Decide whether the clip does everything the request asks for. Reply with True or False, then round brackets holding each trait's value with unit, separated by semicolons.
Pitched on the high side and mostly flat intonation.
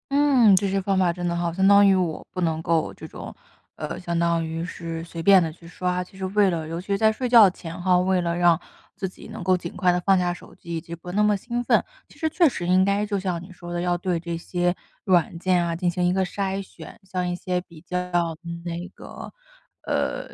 False (180 Hz; 2.1 semitones)